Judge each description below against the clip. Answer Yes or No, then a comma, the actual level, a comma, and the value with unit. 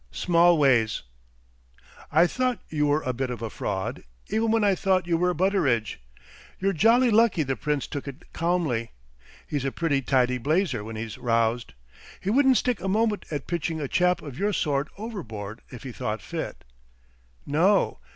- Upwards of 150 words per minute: Yes, average, 170 wpm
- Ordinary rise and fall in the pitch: No, wide, 7.4 semitones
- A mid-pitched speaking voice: Yes, medium, 155 Hz